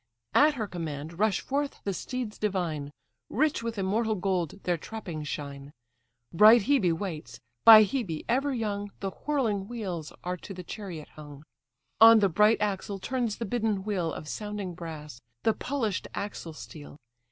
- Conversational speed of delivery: Yes, average, 155 wpm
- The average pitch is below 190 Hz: No, high, 200 Hz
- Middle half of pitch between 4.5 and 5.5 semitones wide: Yes, average, 5.2 semitones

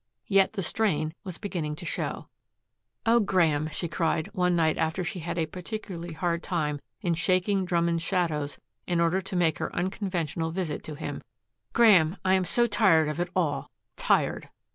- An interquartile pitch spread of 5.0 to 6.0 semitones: No, average, 2.8 semitones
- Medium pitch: Yes, medium, 175 Hz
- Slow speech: No, average, 165 wpm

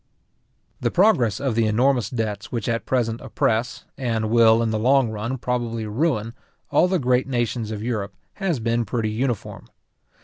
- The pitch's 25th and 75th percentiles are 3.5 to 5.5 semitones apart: No, narrow, 2.4 semitones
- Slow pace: No, average, 165 wpm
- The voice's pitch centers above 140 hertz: No, low, 115 Hz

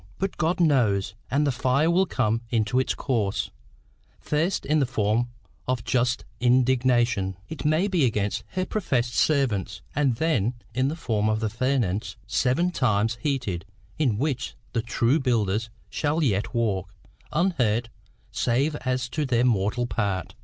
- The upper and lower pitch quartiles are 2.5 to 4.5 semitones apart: No, average, 4.9 semitones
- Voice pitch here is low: Yes, low, 125 Hz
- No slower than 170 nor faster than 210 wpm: No, average, 150 wpm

